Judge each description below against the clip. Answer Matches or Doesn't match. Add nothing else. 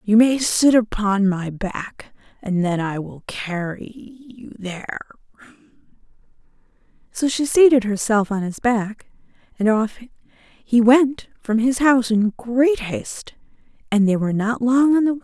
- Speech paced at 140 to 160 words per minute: Matches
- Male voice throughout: Doesn't match